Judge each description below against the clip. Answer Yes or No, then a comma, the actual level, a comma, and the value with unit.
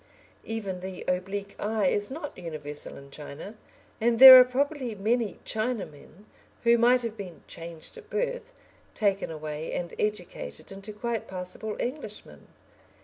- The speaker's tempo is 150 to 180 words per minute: No, average, 140 wpm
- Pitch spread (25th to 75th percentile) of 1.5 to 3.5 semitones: No, average, 4.7 semitones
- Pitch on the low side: No, high, 210 Hz